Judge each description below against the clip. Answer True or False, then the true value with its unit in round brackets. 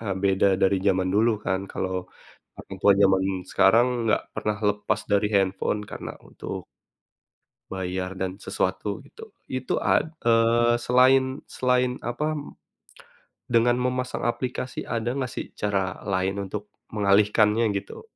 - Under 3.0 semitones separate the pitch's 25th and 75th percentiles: False (4.0 semitones)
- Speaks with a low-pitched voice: True (105 Hz)